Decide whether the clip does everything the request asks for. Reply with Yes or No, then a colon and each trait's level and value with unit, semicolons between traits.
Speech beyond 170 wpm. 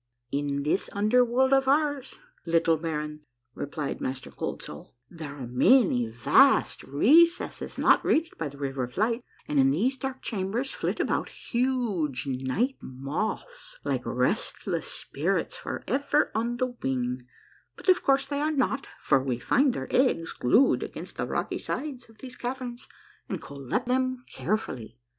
No: average, 155 wpm